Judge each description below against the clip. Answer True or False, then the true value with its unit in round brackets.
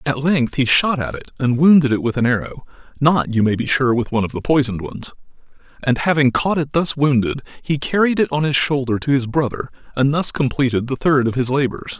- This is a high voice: False (135 Hz)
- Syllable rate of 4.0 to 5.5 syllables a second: False (5.8 syllables/s)